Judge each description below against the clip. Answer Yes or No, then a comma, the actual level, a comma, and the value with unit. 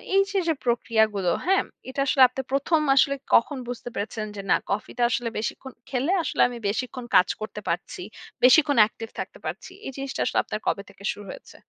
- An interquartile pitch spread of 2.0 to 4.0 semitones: No, average, 4.4 semitones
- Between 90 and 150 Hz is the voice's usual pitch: No, high, 245 Hz